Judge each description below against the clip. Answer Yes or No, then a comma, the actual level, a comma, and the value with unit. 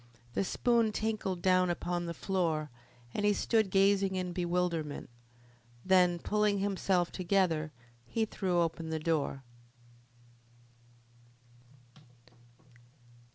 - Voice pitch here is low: No, medium, 185 Hz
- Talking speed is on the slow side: Yes, slow, 100 wpm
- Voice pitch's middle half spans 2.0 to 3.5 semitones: Yes, average, 2.7 semitones